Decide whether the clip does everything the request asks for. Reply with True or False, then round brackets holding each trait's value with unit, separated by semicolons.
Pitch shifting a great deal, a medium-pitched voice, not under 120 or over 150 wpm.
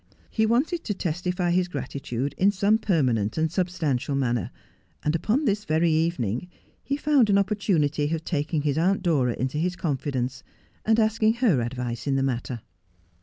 False (6.7 semitones; 165 Hz; 170 wpm)